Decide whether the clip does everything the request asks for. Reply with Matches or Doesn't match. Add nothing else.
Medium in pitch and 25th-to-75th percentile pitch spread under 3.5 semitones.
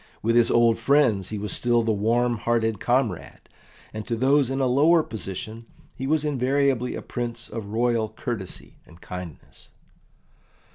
Doesn't match